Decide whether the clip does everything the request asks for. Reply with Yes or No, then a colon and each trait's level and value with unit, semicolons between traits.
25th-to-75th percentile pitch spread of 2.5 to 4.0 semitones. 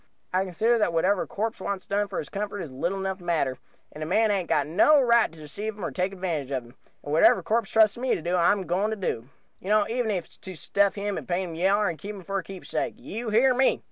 Yes: average, 3.6 semitones